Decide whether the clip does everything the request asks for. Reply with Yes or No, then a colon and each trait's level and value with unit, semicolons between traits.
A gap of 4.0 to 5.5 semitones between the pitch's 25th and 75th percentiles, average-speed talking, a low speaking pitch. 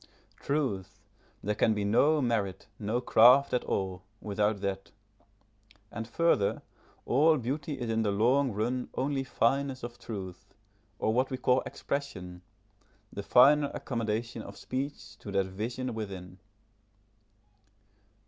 No: average, 4.6 semitones; slow, 130 wpm; low, 115 Hz